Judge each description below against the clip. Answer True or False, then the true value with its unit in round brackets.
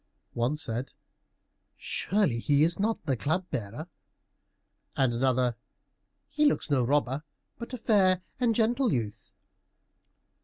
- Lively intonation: True (8.7 semitones)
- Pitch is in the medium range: True (150 Hz)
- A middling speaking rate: False (120 wpm)